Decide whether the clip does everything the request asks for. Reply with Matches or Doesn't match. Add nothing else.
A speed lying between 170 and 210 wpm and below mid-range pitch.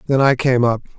Doesn't match